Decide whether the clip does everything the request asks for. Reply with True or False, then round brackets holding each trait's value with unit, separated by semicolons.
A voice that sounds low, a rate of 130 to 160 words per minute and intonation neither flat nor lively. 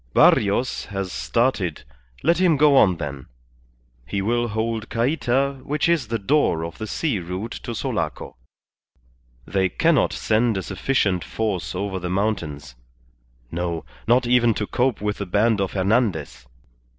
True (110 Hz; 145 wpm; 4.9 semitones)